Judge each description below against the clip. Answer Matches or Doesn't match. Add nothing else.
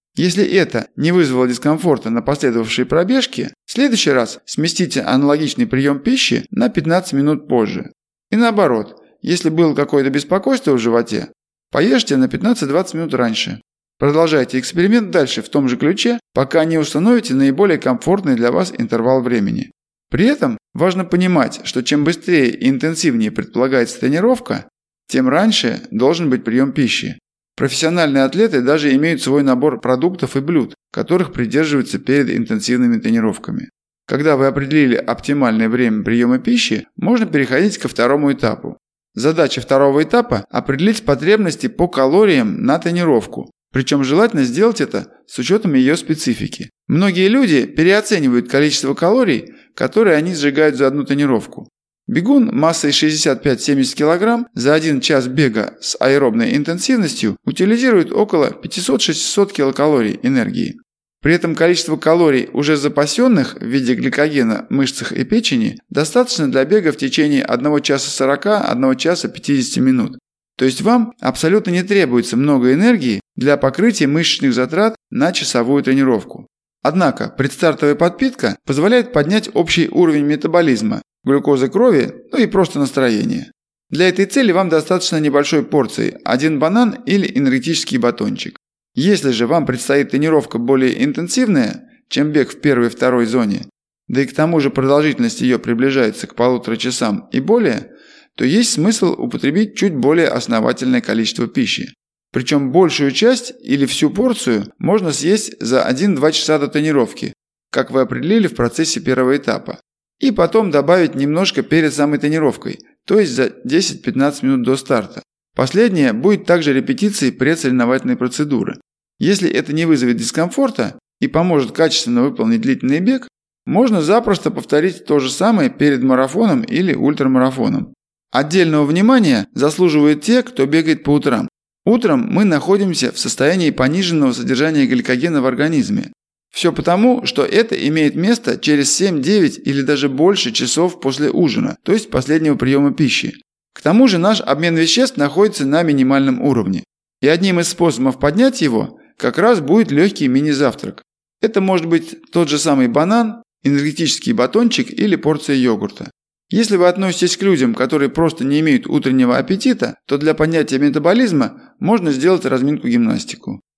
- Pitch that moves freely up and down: Matches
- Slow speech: Doesn't match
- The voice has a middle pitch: Matches